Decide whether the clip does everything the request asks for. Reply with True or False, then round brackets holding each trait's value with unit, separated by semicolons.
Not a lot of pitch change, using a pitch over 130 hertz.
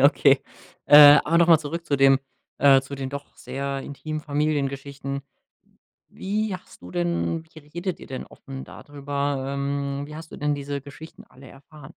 True (1.8 semitones; 140 Hz)